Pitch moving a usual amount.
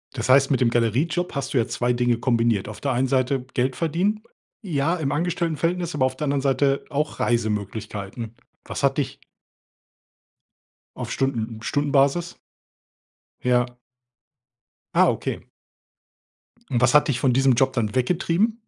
Yes: average, 3.8 semitones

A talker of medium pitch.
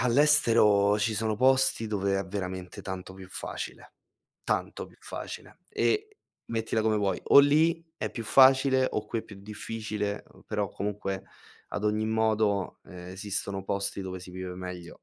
No: low, 105 Hz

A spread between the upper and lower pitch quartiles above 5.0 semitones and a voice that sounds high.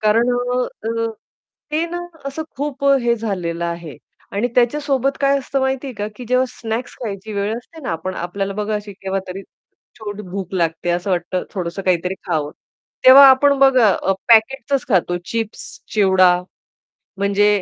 Yes: wide, 5.4 semitones; high, 215 Hz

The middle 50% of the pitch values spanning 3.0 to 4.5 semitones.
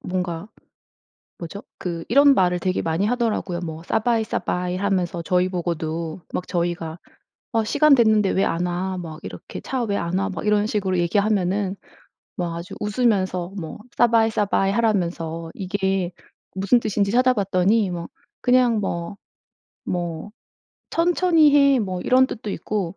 Yes: average, 3.9 semitones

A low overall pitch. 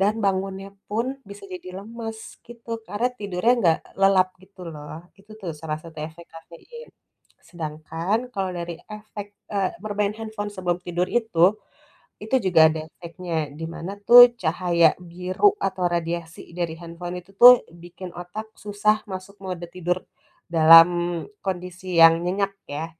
No: medium, 185 Hz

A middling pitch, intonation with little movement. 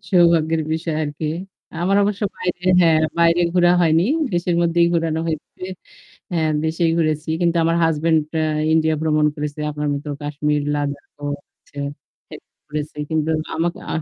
Yes: medium, 160 Hz; narrow, 2.0 semitones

